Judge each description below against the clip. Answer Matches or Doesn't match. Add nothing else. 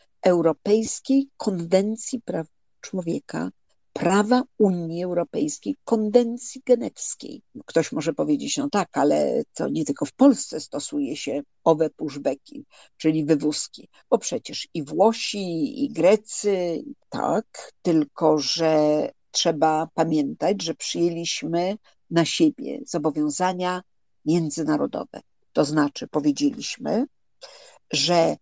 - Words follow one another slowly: Matches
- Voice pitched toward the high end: Doesn't match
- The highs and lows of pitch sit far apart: Matches